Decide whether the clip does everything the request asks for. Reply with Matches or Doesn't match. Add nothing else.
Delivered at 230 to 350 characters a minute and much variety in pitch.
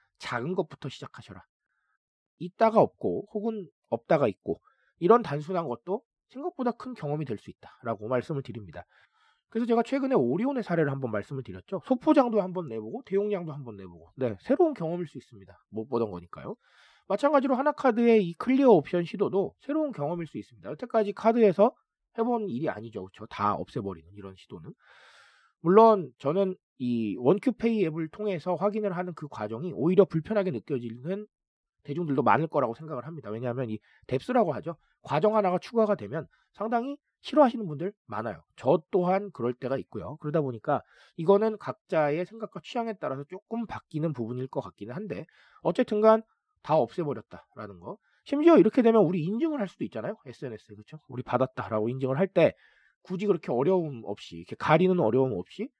Doesn't match